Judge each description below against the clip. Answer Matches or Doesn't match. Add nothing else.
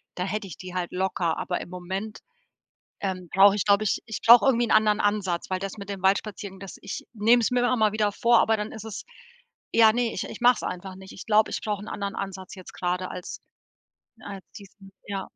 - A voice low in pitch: Doesn't match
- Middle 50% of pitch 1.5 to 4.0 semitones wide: Matches